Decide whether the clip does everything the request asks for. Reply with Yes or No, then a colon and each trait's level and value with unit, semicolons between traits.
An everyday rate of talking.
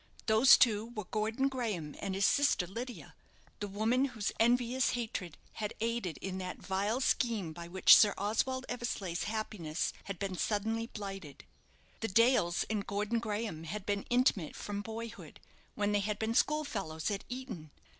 Yes: average, 160 wpm